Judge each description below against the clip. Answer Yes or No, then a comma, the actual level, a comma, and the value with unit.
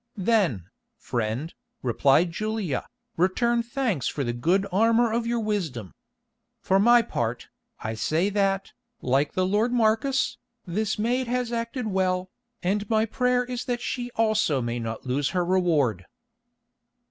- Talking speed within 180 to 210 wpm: No, average, 140 wpm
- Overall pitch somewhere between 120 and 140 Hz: No, high, 195 Hz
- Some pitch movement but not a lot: No, wide, 8.1 semitones